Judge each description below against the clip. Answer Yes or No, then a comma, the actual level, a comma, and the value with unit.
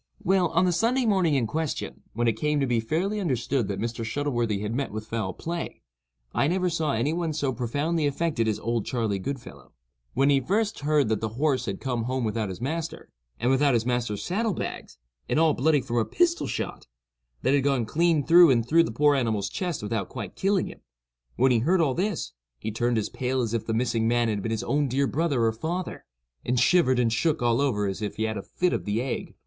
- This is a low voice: Yes, low, 130 Hz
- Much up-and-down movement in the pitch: Yes, wide, 5.9 semitones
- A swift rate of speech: Yes, fast, 230 wpm